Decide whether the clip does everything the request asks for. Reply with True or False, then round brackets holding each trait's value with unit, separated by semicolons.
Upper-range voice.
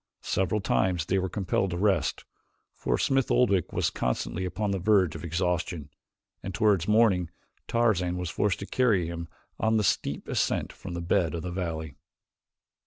False (90 Hz)